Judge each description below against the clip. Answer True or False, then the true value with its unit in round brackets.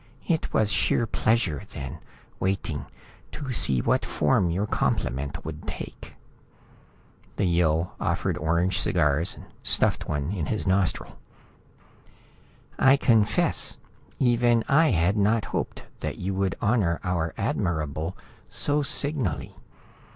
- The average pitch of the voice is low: True (95 Hz)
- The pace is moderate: False (115 wpm)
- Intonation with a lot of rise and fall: True (6.1 semitones)